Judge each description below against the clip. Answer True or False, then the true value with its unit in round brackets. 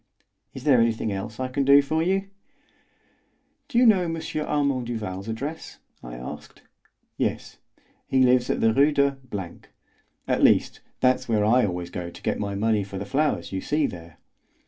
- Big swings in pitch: True (6.0 semitones)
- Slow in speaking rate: False (170 wpm)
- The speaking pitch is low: True (125 Hz)